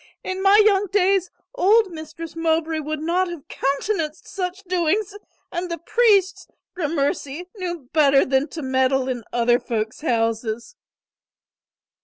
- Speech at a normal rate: No, slow, 130 wpm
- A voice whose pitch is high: Yes, very high, 330 Hz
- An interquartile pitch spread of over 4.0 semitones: Yes, wide, 5.5 semitones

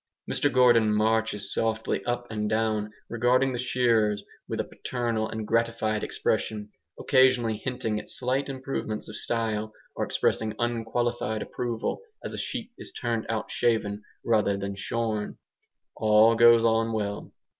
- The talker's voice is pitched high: No, low, 115 Hz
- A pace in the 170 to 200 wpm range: No, average, 140 wpm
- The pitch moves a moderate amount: No, narrow, 1.9 semitones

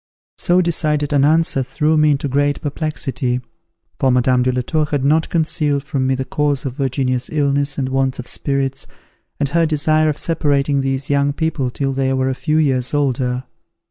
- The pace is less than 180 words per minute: No, average, 185 wpm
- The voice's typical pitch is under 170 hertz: Yes, medium, 140 Hz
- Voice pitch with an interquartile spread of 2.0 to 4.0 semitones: Yes, narrow, 2.4 semitones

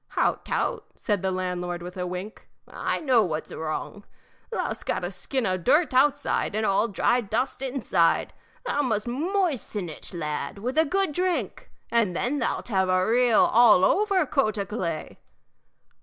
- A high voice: Yes, high, 220 Hz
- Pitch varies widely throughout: Yes, wide, 6.6 semitones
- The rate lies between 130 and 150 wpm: No, average, 170 wpm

